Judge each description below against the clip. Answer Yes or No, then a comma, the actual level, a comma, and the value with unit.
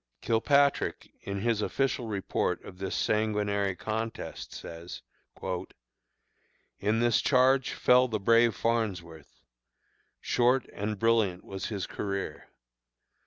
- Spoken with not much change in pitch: No, average, 3.3 semitones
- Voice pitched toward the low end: Yes, low, 110 Hz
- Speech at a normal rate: No, slow, 105 wpm